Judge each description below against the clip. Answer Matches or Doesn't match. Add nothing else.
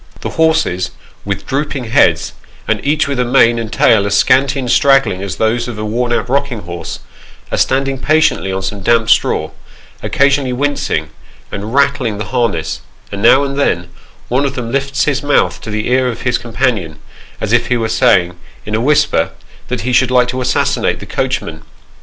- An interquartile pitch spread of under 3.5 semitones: Doesn't match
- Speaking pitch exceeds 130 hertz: Doesn't match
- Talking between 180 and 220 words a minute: Matches